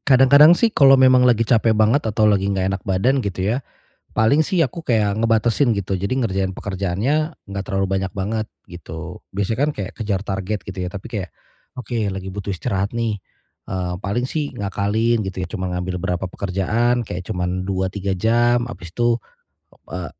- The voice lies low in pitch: Yes, low, 105 Hz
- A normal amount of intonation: Yes, average, 3.9 semitones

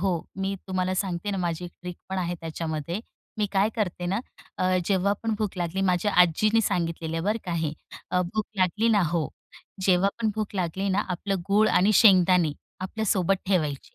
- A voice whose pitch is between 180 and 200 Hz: Yes, medium, 185 Hz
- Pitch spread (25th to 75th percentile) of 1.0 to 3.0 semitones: Yes, narrow, 2.6 semitones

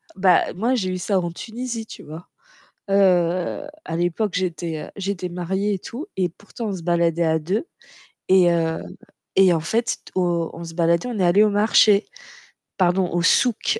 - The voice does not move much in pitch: No, average, 3.2 semitones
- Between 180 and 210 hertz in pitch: Yes, medium, 185 Hz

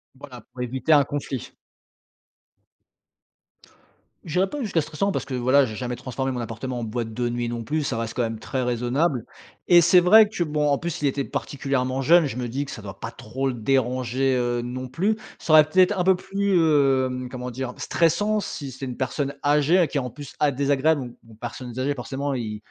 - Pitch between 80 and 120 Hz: No, low, 135 Hz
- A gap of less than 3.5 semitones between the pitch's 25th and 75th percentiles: No, average, 3.8 semitones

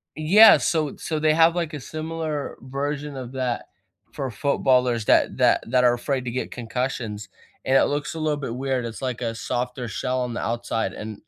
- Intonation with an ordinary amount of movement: Yes, average, 3.6 semitones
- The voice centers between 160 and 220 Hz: No, low, 130 Hz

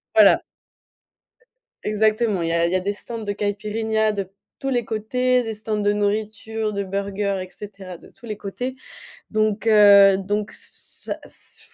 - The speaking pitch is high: Yes, high, 210 Hz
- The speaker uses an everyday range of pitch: No, narrow, 1.7 semitones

